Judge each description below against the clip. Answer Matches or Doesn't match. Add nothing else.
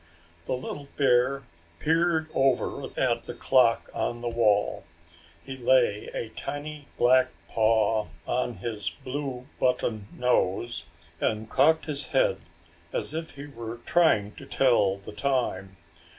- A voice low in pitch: Matches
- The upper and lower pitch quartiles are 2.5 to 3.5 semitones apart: Doesn't match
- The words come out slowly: Matches